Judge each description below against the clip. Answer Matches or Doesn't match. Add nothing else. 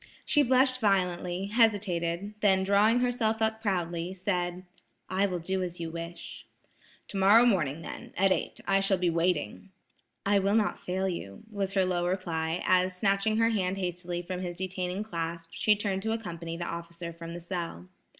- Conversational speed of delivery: Matches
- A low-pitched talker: Doesn't match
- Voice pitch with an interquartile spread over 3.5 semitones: Doesn't match